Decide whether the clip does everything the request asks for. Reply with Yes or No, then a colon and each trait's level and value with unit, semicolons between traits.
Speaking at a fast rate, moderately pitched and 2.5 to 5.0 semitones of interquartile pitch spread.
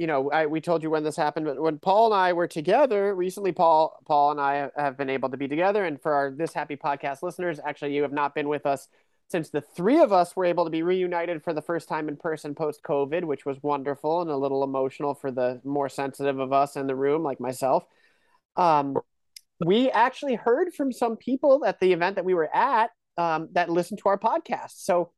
Yes: fast, 235 wpm; medium, 160 Hz; average, 4.1 semitones